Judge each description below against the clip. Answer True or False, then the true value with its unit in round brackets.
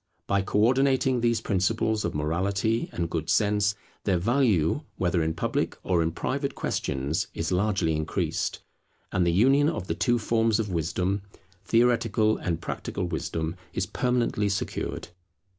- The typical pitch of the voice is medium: False (100 Hz)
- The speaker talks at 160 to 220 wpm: False (145 wpm)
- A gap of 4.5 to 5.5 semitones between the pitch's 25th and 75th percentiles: True (5.2 semitones)